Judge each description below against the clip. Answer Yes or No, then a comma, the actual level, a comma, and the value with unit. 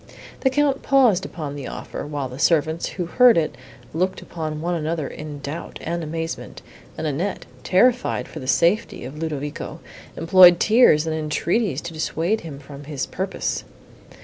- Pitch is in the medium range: Yes, medium, 165 Hz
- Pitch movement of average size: Yes, average, 3.7 semitones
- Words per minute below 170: Yes, average, 160 wpm